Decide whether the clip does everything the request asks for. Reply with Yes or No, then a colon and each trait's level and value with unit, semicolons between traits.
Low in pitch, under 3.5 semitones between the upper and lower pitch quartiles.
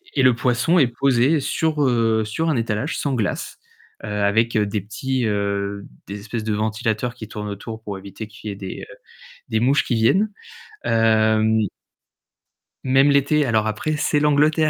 No: low, 115 Hz; average, 4.3 semitones